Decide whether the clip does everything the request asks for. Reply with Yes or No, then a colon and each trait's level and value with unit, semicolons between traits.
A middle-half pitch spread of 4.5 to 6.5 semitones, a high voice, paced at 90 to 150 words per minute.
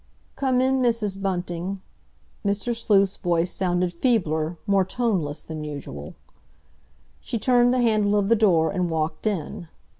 Yes: average, 5.1 semitones; high, 195 Hz; average, 140 wpm